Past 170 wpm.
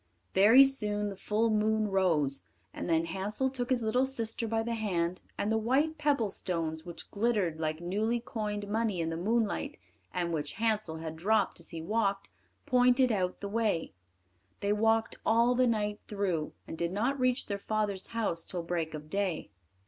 Yes: average, 180 wpm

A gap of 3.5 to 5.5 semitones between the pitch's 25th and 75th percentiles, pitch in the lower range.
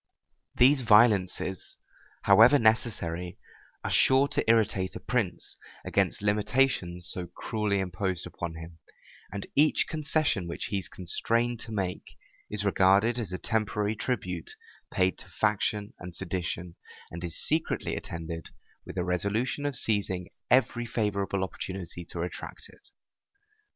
Yes: average, 4.3 semitones; low, 100 Hz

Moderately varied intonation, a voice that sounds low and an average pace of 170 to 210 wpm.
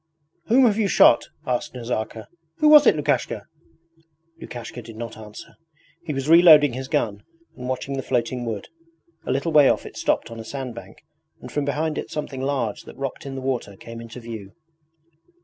Yes: average, 4.1 semitones; low, 130 Hz; average, 185 wpm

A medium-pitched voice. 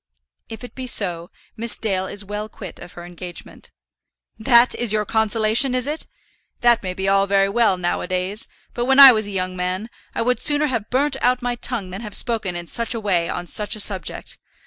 No: high, 215 Hz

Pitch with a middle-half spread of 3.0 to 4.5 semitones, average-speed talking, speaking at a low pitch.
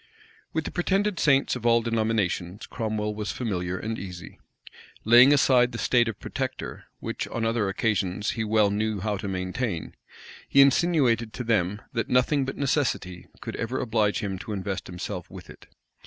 Yes: average, 4.1 semitones; average, 170 wpm; low, 110 Hz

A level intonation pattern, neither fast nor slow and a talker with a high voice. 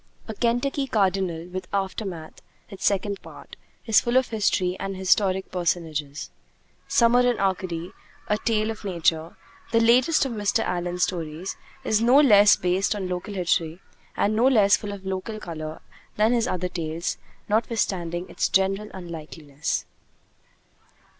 No: average, 4.0 semitones; average, 145 wpm; high, 195 Hz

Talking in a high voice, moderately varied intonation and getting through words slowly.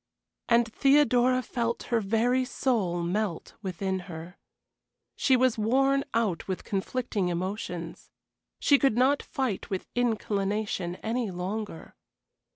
Yes: high, 220 Hz; average, 5.0 semitones; slow, 115 wpm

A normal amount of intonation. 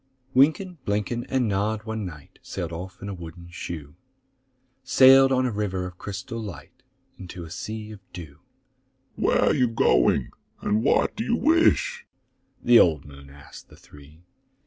No: wide, 6.9 semitones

